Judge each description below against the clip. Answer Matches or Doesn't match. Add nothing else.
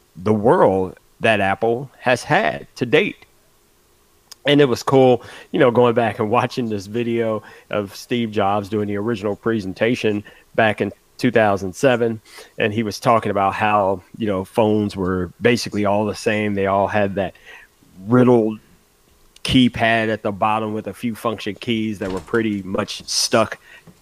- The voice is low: Matches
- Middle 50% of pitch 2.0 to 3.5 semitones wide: Matches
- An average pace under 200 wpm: Matches